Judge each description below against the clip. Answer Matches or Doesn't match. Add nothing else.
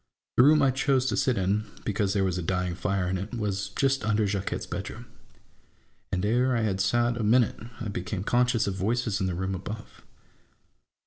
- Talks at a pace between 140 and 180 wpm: Doesn't match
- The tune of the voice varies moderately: Matches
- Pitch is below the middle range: Matches